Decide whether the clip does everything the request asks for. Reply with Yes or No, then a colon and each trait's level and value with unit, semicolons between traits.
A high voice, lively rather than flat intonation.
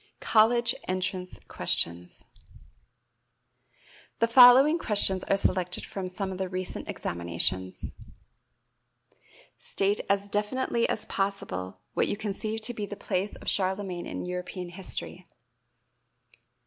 No: high, 195 Hz; average, 3.0 semitones